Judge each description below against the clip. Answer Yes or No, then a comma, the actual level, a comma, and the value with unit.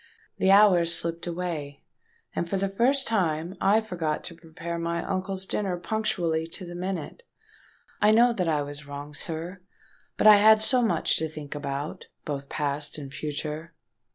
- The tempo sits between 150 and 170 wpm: Yes, average, 160 wpm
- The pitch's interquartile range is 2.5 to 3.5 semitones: No, average, 4.2 semitones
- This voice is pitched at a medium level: Yes, medium, 170 Hz